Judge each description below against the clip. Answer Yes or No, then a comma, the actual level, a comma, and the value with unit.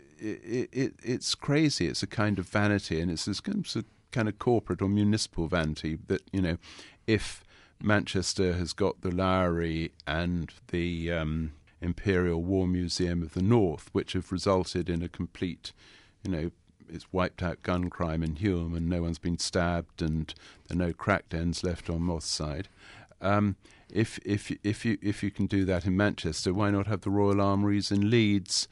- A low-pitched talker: Yes, very low, 95 Hz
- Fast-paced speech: No, average, 180 wpm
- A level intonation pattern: No, average, 3.0 semitones